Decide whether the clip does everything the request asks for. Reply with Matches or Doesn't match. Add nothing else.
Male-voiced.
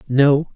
Matches